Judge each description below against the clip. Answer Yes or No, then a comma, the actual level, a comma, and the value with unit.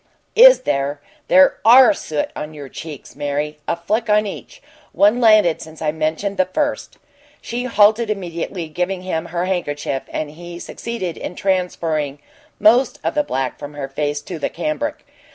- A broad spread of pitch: Yes, wide, 6.1 semitones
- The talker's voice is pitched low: No, medium, 175 Hz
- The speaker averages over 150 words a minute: Yes, average, 165 wpm